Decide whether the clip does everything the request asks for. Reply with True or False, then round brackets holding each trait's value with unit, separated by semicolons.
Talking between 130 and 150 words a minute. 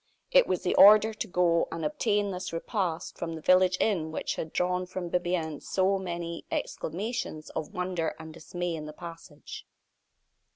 False (165 wpm)